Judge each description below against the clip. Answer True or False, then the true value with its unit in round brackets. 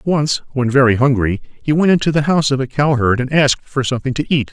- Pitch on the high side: False (135 Hz)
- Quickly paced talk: True (240 wpm)